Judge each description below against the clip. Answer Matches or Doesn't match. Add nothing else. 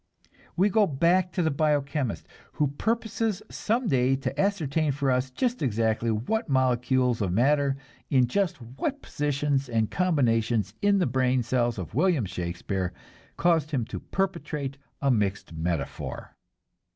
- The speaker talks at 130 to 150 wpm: Matches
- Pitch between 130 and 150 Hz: Matches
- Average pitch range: Doesn't match